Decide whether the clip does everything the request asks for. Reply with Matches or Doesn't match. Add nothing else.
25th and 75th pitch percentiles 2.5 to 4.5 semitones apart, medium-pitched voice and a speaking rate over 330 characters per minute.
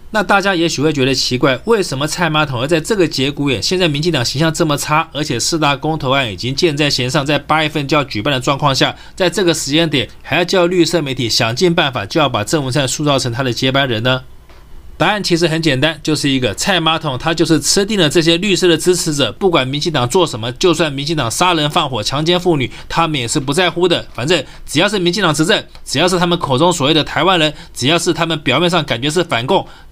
Matches